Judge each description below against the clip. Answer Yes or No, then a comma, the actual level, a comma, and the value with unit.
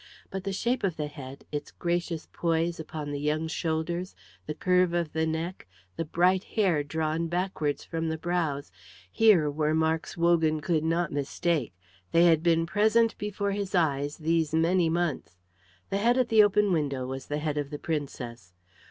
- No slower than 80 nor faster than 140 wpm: No, average, 175 wpm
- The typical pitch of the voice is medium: Yes, medium, 165 Hz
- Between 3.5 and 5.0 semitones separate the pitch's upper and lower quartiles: No, average, 2.9 semitones